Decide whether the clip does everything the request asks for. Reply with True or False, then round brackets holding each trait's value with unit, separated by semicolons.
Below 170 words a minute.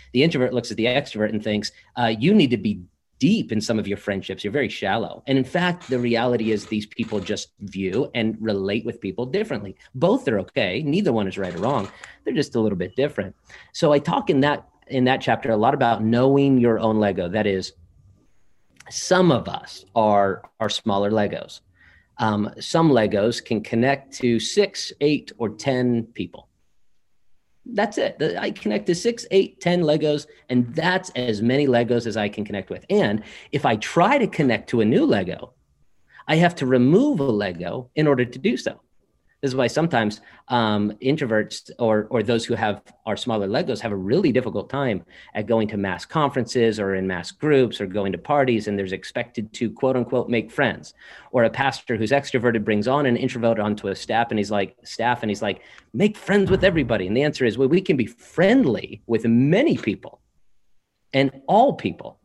False (200 wpm)